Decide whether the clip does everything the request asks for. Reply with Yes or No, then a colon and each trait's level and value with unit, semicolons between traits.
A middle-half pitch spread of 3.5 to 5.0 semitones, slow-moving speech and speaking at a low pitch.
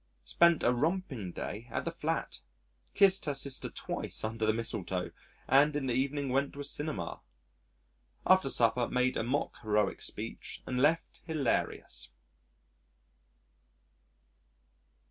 Yes: average, 4.3 semitones; slow, 125 wpm; low, 130 Hz